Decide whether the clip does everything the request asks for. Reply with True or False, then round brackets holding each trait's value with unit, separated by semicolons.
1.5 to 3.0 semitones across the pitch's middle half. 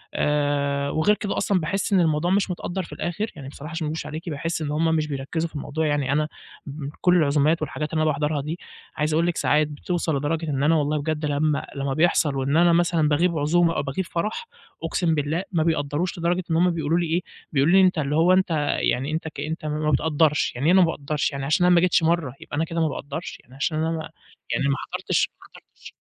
True (2.6 semitones)